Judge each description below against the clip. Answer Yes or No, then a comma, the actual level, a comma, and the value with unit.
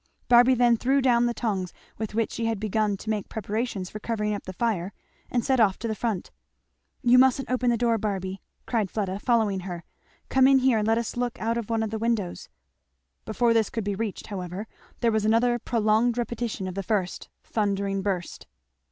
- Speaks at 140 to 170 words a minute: No, fast, 205 wpm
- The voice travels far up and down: No, average, 2.9 semitones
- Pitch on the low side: No, high, 220 Hz